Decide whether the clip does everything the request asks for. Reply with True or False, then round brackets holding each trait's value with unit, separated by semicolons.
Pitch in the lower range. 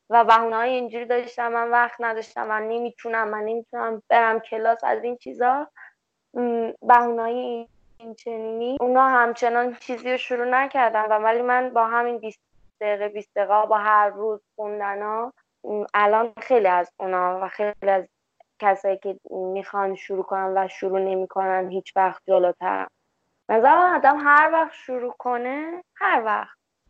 False (225 Hz)